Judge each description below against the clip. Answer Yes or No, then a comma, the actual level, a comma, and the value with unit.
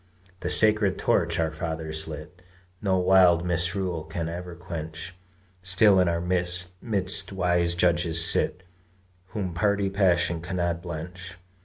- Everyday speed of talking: No, slow, 125 wpm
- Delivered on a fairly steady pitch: Yes, narrow, 1.7 semitones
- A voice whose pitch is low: Yes, very low, 90 Hz